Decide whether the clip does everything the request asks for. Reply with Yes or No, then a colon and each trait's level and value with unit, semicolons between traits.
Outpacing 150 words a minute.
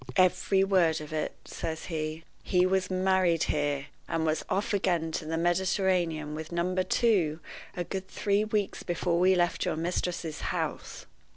Yes: average, 160 wpm